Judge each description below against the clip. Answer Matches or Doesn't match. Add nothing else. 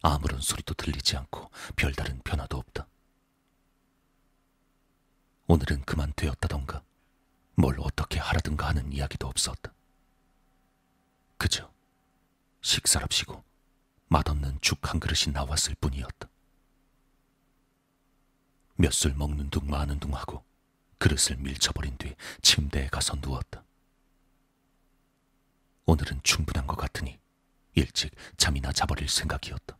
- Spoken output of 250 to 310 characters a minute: Doesn't match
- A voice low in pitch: Matches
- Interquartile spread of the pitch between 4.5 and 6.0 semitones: Doesn't match